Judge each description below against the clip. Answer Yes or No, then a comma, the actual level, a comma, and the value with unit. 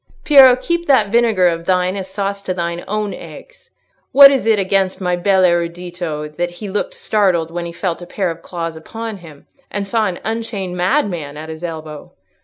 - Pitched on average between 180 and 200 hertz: Yes, medium, 185 Hz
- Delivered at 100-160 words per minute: No, average, 195 wpm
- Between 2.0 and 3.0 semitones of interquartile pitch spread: No, average, 3.7 semitones